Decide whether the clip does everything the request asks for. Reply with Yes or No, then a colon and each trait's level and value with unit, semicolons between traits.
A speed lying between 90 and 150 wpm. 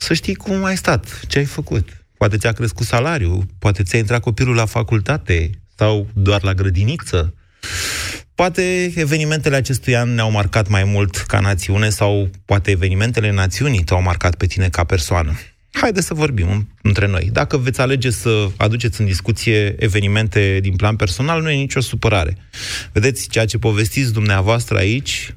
No: average, 160 wpm